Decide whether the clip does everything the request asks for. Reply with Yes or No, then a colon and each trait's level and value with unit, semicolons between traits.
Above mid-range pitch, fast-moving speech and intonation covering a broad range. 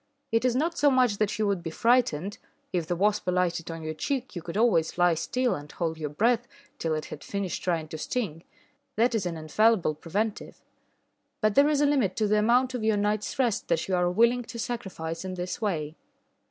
Yes: high, 200 Hz; fast, 215 wpm; wide, 5.9 semitones